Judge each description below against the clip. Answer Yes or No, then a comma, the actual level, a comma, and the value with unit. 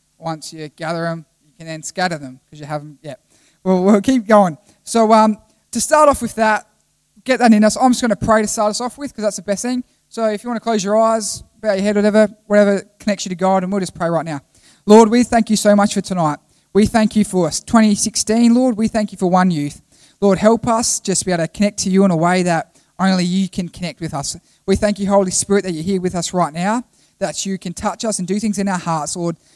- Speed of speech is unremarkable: No, fast, 270 wpm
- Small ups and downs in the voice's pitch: No, average, 4.0 semitones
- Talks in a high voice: Yes, high, 200 Hz